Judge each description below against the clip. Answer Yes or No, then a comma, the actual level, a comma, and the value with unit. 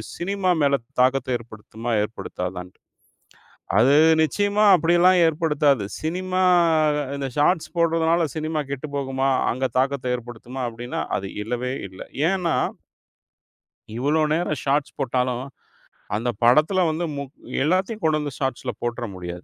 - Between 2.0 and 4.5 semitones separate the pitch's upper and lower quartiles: No, average, 5.1 semitones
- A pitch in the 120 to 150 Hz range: Yes, medium, 140 Hz